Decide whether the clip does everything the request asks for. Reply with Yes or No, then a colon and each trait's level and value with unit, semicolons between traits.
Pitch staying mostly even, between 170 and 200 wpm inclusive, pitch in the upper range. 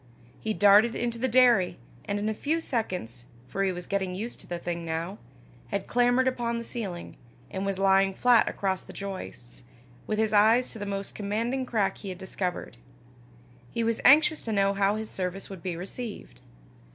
No: average, 3.7 semitones; average, 190 wpm; high, 200 Hz